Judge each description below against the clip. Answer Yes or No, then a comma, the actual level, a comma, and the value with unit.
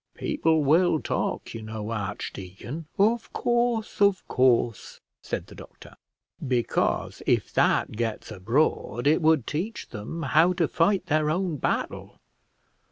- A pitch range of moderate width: No, wide, 7.5 semitones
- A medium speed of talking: No, slow, 130 wpm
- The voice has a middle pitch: Yes, medium, 155 Hz